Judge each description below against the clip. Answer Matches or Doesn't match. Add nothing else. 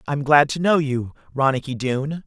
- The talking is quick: Doesn't match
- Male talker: Matches